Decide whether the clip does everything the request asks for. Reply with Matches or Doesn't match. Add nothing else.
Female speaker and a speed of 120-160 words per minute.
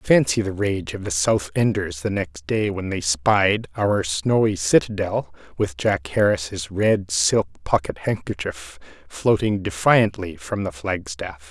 Doesn't match